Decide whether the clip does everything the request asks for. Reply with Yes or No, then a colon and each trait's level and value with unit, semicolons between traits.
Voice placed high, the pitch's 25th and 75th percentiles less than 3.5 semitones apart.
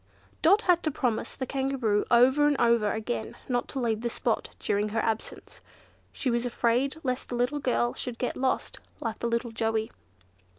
Yes: high, 240 Hz; average, 2.9 semitones